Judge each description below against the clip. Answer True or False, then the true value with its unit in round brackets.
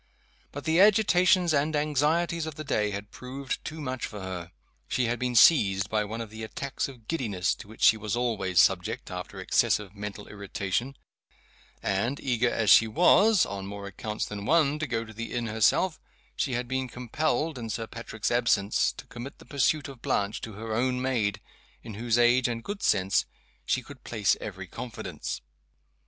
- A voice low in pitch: True (120 Hz)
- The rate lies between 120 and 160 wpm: False (185 wpm)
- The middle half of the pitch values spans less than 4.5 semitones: False (4.9 semitones)